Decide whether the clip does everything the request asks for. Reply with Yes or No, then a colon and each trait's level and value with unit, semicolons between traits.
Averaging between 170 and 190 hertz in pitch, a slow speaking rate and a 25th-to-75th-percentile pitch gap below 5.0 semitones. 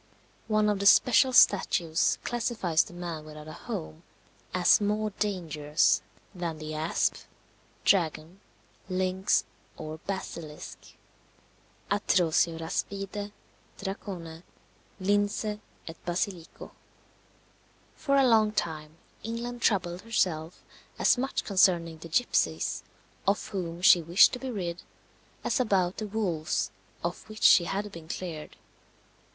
Yes: medium, 185 Hz; slow, 115 wpm; average, 4.2 semitones